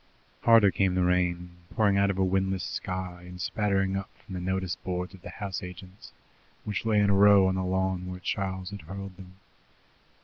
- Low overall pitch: Yes, very low, 95 Hz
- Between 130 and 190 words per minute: No, average, 200 wpm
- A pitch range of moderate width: No, narrow, 1.4 semitones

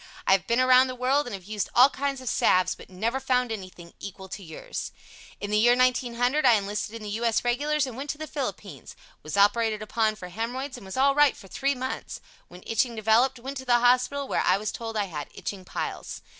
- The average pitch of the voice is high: Yes, high, 235 Hz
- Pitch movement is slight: No, average, 4.0 semitones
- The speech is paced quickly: Yes, fast, 230 wpm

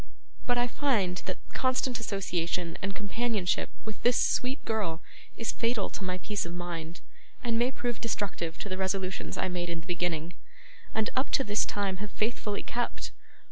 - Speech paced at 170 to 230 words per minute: Yes, average, 175 wpm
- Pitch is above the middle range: Yes, high, 200 Hz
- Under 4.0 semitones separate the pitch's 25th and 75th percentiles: No, average, 4.7 semitones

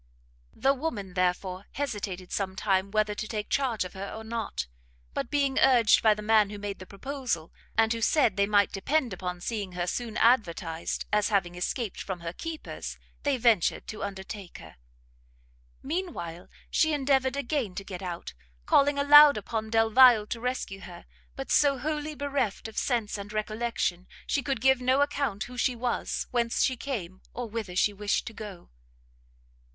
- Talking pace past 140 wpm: Yes, average, 175 wpm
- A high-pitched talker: Yes, high, 220 Hz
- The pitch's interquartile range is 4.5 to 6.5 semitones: Yes, average, 5.2 semitones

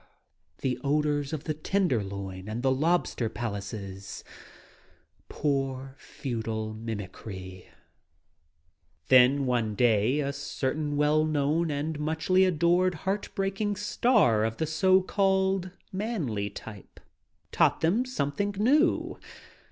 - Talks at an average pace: No, slow, 110 wpm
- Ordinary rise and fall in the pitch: No, wide, 8.4 semitones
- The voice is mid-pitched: Yes, medium, 145 Hz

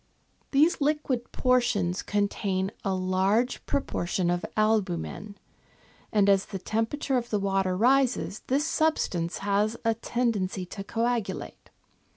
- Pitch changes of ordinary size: Yes, average, 4.3 semitones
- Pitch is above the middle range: Yes, high, 210 Hz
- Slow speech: Yes, slow, 125 wpm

